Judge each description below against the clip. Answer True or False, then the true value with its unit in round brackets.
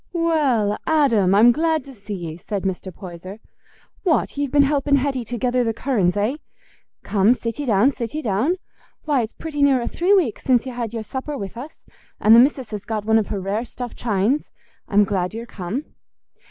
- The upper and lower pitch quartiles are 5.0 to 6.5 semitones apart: True (5.4 semitones)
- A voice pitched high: True (235 Hz)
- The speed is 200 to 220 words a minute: True (205 wpm)